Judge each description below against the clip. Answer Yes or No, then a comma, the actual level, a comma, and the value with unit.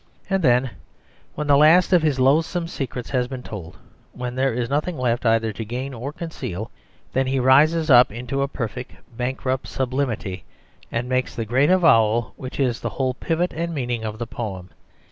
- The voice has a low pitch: Yes, low, 130 Hz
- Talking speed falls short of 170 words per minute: No, average, 185 wpm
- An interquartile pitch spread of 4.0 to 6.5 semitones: No, average, 3.3 semitones